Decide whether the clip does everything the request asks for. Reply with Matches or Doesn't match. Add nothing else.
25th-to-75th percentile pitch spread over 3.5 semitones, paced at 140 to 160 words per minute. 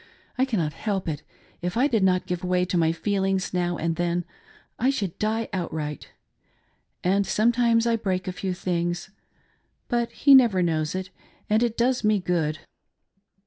Doesn't match